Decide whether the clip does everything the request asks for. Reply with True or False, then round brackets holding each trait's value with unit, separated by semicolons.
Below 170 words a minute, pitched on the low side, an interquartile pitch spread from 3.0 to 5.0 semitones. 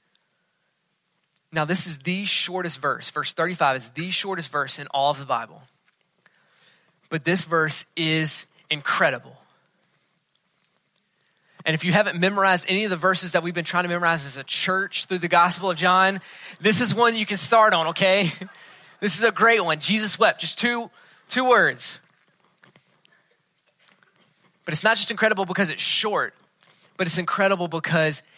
False (160 wpm; 180 Hz; 3.3 semitones)